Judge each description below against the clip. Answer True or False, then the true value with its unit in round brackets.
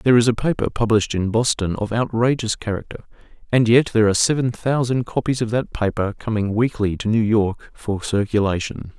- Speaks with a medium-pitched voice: False (110 Hz)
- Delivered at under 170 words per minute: False (180 wpm)